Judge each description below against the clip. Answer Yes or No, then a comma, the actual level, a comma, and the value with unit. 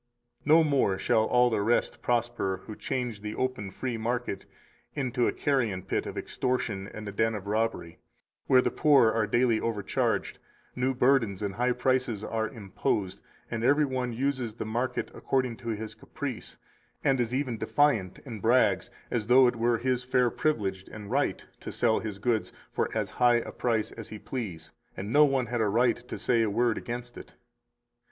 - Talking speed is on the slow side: No, average, 185 wpm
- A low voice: Yes, low, 120 Hz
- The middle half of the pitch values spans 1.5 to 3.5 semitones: Yes, average, 2.9 semitones